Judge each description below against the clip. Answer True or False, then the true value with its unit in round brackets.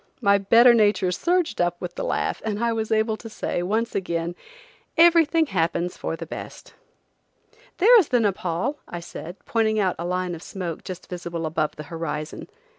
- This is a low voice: False (190 Hz)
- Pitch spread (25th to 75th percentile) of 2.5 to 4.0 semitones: False (4.8 semitones)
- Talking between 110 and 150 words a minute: False (180 wpm)